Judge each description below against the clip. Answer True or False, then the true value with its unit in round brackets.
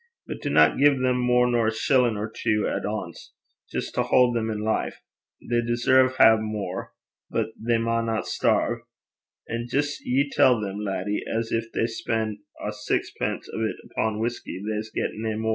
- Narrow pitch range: True (2.1 semitones)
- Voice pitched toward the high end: False (115 Hz)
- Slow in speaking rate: False (180 wpm)